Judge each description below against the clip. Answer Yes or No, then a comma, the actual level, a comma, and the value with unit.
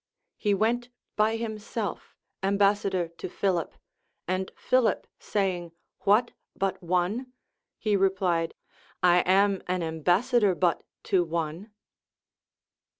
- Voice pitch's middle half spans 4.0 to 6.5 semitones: No, average, 3.1 semitones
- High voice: Yes, high, 195 Hz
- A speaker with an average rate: No, slow, 105 wpm